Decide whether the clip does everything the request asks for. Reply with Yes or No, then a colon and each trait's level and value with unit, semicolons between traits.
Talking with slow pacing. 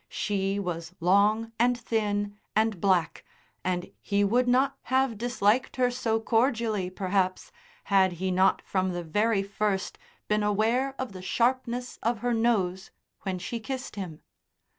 No: average, 145 wpm